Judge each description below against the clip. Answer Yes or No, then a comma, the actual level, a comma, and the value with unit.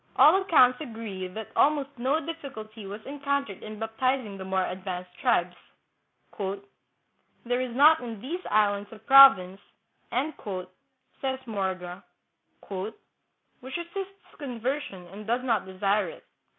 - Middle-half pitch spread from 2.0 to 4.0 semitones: No, wide, 5.6 semitones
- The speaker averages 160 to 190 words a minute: No, slow, 135 wpm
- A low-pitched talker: No, high, 225 Hz